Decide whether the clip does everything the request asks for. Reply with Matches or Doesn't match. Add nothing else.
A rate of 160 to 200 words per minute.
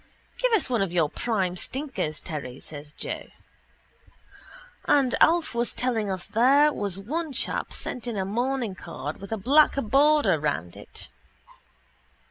Doesn't match